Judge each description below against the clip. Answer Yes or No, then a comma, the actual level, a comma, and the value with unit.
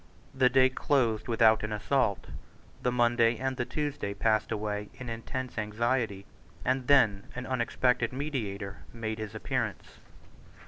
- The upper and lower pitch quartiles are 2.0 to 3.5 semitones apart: Yes, average, 3.1 semitones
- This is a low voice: Yes, low, 120 Hz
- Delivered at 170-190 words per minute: No, slow, 135 wpm